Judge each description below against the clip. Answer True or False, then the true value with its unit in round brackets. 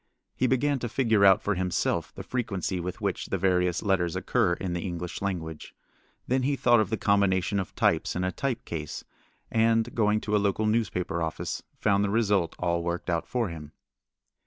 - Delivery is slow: False (190 wpm)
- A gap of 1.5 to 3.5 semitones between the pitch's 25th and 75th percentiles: False (4.2 semitones)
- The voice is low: True (100 Hz)